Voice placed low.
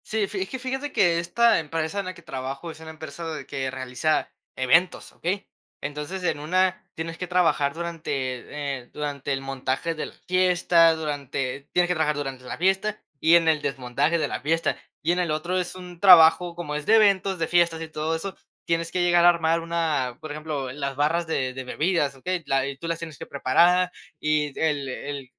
No: medium, 160 Hz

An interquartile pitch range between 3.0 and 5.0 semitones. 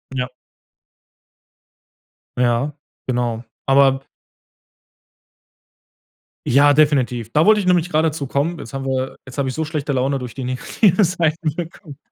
Yes: average, 3.6 semitones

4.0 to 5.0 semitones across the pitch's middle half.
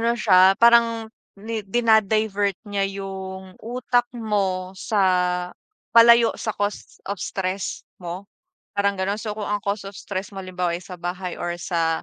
No: average, 2.9 semitones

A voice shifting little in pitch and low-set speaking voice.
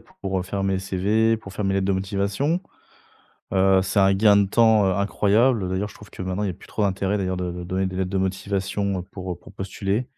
Yes: narrow, 1.5 semitones; very low, 95 Hz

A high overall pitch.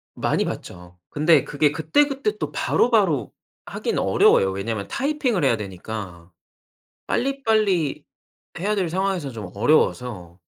No: medium, 150 Hz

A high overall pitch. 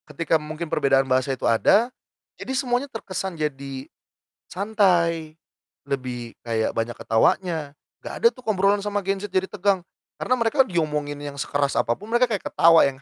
No: medium, 170 Hz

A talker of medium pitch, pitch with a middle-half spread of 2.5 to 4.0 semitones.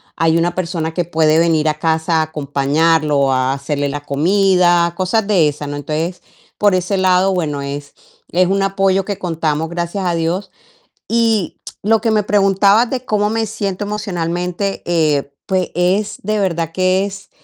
Yes: medium, 175 Hz; average, 3.7 semitones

